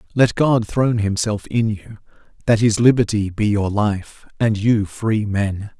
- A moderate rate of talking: Yes, average, 165 wpm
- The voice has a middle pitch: No, low, 105 Hz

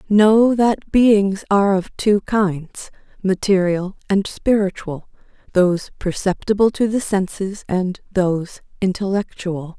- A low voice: No, high, 195 Hz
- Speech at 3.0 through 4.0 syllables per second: Yes, 3.9 syllables/s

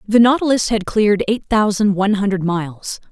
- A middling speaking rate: Yes, average, 175 wpm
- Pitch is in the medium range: No, high, 205 Hz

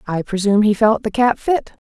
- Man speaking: No, female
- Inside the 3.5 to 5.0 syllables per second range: No, 5.6 syllables/s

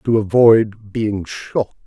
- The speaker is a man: Yes, male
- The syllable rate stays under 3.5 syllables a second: Yes, 3.0 syllables/s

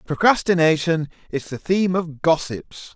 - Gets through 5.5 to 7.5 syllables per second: No, 4.6 syllables/s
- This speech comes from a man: Yes, male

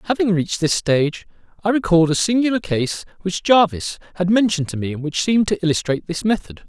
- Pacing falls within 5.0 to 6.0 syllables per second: No, 6.5 syllables/s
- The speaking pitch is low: No, medium, 180 Hz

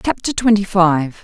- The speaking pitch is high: Yes, high, 195 Hz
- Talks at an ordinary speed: Yes, average, 145 wpm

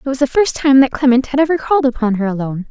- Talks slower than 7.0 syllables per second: No, 7.1 syllables/s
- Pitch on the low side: No, very high, 260 Hz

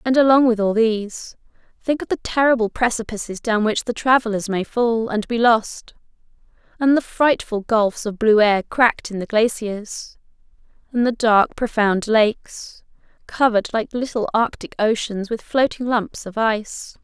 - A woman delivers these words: Yes, female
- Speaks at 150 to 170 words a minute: Yes, average, 160 wpm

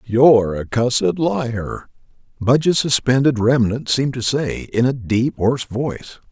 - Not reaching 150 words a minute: Yes, average, 140 wpm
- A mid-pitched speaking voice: No, low, 125 Hz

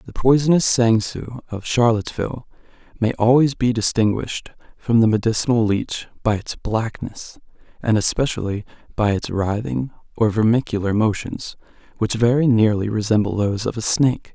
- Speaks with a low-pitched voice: Yes, low, 115 Hz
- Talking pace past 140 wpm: No, slow, 135 wpm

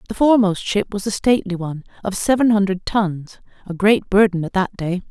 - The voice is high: Yes, high, 200 Hz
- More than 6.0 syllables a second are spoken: No, 5.7 syllables/s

